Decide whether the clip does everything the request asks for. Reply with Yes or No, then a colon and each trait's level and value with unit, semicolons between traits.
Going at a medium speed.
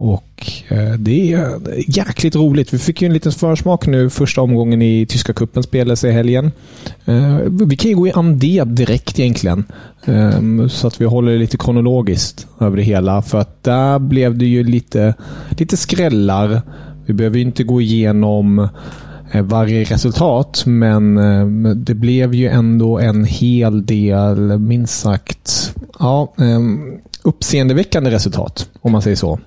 Yes: average, 145 wpm